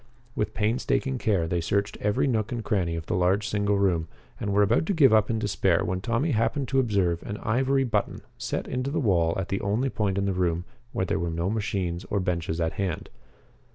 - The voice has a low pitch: Yes, low, 100 Hz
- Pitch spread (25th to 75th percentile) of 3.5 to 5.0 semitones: Yes, average, 4.4 semitones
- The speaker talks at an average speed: No, fast, 220 wpm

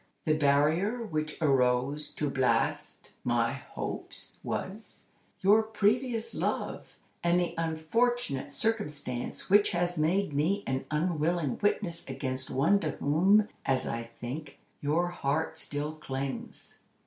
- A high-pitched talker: No, medium, 155 Hz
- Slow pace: Yes, slow, 120 wpm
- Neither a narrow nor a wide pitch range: No, wide, 5.9 semitones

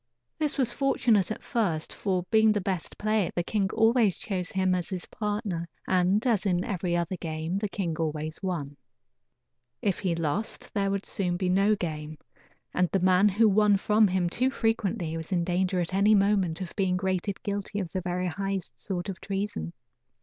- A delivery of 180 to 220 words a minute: Yes, average, 185 wpm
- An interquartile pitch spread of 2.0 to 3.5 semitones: Yes, average, 2.9 semitones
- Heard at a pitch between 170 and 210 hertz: Yes, high, 190 Hz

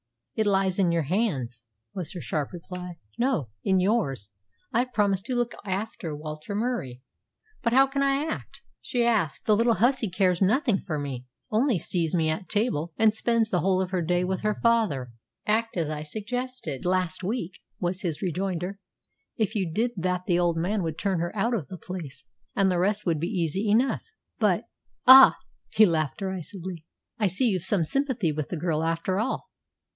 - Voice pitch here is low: No, medium, 185 Hz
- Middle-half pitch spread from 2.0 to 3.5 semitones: No, average, 4.9 semitones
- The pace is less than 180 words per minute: No, average, 190 wpm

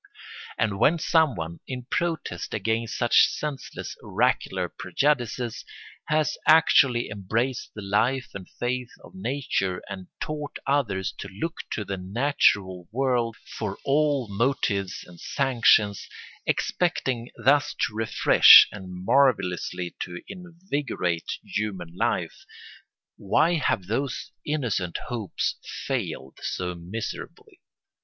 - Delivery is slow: Yes, slow, 110 wpm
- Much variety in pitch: Yes, wide, 6.4 semitones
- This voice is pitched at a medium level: No, low, 115 Hz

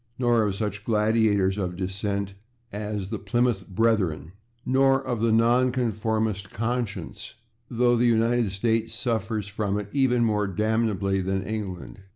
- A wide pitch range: No, average, 2.9 semitones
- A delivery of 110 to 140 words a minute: Yes, slow, 135 wpm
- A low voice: Yes, low, 110 Hz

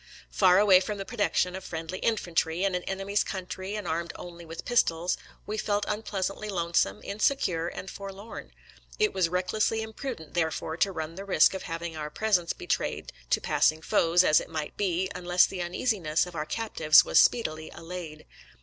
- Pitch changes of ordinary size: Yes, average, 3.5 semitones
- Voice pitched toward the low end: No, medium, 180 Hz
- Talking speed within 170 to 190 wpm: Yes, average, 175 wpm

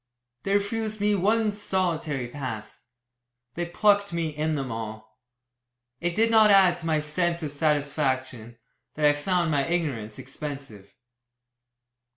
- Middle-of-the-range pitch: Yes, medium, 155 Hz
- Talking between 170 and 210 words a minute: No, slow, 135 wpm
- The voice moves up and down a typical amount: No, wide, 5.8 semitones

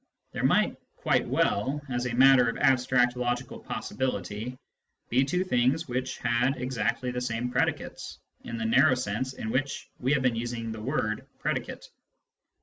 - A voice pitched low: Yes, low, 125 Hz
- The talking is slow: No, average, 165 wpm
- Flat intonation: Yes, narrow, 2.1 semitones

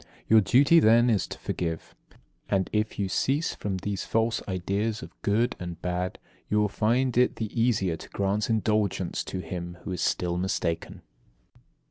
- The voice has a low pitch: Yes, low, 100 Hz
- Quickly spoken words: No, average, 165 wpm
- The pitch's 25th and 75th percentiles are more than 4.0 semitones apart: No, average, 3.7 semitones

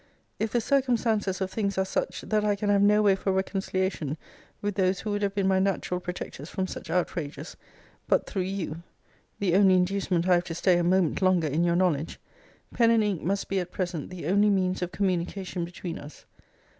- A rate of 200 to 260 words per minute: Yes, fast, 205 wpm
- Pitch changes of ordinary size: No, narrow, 2.3 semitones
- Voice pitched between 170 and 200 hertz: Yes, high, 190 Hz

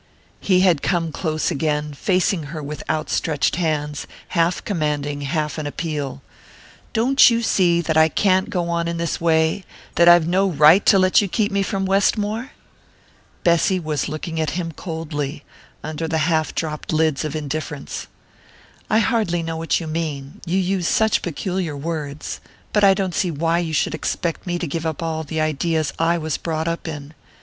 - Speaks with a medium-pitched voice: Yes, medium, 165 Hz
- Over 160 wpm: Yes, average, 175 wpm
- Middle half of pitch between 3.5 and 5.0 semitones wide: No, average, 2.9 semitones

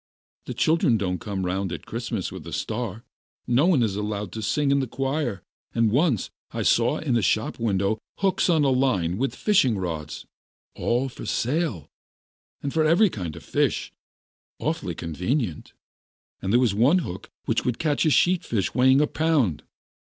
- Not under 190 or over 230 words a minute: No, average, 175 wpm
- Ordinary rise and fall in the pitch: No, wide, 6.6 semitones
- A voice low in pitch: Yes, low, 120 Hz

